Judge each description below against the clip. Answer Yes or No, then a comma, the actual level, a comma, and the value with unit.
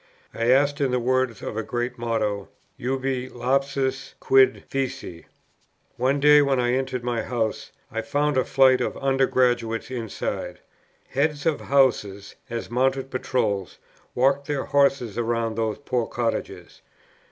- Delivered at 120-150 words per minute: Yes, average, 140 wpm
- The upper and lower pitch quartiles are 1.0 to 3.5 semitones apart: Yes, narrow, 2.6 semitones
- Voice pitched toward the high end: No, low, 130 Hz